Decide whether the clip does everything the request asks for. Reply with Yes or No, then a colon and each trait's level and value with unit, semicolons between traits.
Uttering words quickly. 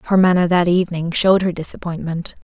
No: average, 165 wpm